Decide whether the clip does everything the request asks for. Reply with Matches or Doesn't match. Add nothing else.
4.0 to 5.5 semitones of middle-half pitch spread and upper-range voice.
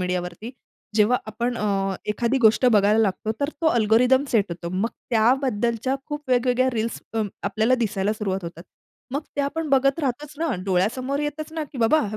Matches